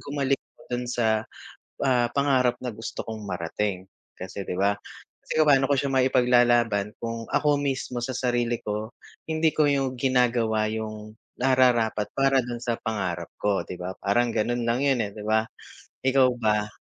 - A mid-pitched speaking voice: No, low, 120 Hz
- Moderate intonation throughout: Yes, average, 3.4 semitones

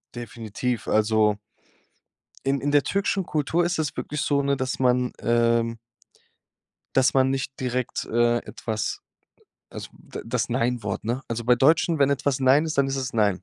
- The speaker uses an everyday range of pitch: Yes, average, 3.1 semitones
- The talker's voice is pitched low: Yes, low, 125 Hz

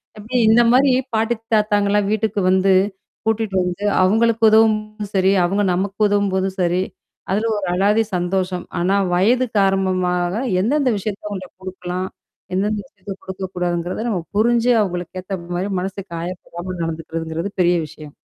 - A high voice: Yes, high, 195 Hz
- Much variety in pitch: No, average, 2.8 semitones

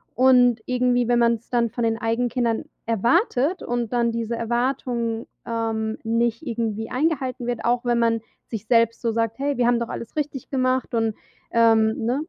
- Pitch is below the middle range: No, high, 235 Hz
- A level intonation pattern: Yes, narrow, 1.5 semitones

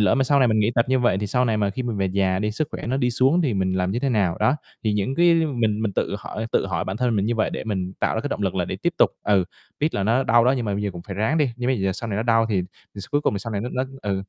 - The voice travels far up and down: No, average, 4.2 semitones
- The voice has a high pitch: No, low, 110 Hz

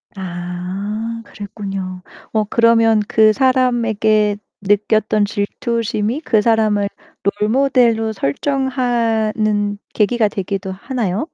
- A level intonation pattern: Yes, narrow, 2.2 semitones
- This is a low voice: No, high, 215 Hz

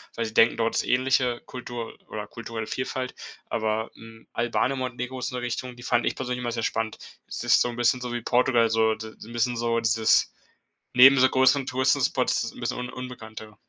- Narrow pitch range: Yes, narrow, 2.0 semitones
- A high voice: No, low, 120 Hz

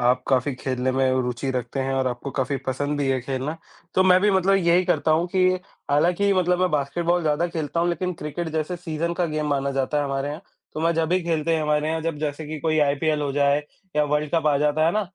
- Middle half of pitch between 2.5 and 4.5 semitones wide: Yes, average, 3.4 semitones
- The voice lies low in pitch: No, medium, 150 Hz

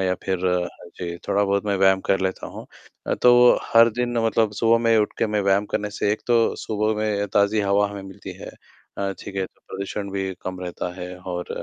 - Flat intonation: Yes, narrow, 2.0 semitones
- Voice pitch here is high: No, low, 100 Hz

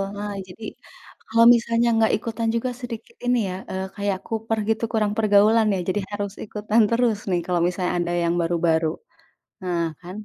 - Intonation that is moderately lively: Yes, average, 3.8 semitones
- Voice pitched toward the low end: No, high, 210 Hz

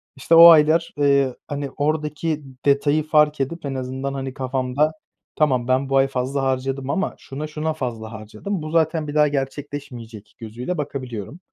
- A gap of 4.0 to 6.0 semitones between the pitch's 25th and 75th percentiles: No, average, 2.7 semitones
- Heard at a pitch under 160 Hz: Yes, medium, 140 Hz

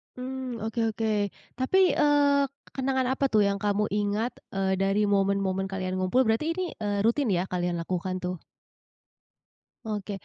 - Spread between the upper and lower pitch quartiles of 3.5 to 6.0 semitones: Yes, average, 5.1 semitones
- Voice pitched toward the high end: Yes, high, 210 Hz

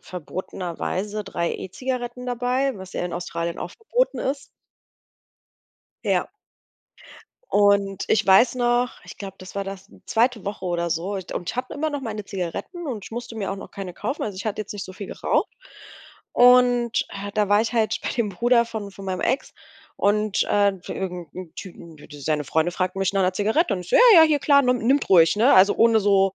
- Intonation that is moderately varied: Yes, average, 4.5 semitones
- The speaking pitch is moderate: No, high, 205 Hz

